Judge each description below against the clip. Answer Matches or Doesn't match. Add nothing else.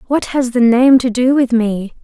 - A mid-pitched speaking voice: Doesn't match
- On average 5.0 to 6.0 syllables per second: Doesn't match